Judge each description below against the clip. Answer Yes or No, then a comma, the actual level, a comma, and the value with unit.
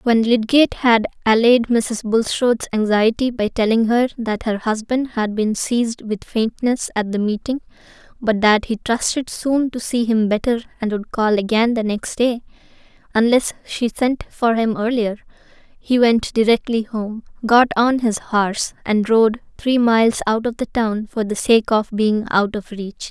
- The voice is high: Yes, high, 225 Hz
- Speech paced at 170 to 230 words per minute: Yes, average, 175 wpm